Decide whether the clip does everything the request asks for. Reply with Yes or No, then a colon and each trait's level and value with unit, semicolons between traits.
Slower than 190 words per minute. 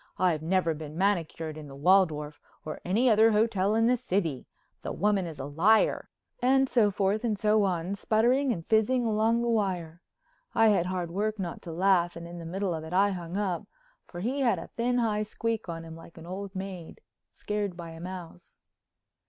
No: average, 195 wpm